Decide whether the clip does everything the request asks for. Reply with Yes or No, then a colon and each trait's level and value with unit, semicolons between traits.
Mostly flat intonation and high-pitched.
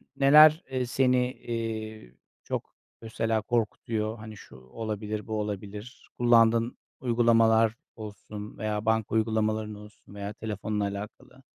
No: narrow, 1.7 semitones; low, 110 Hz